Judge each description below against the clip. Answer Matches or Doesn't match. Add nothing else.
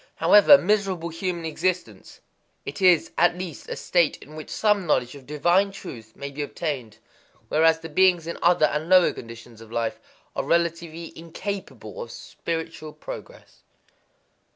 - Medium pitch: Matches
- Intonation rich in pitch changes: Doesn't match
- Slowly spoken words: Doesn't match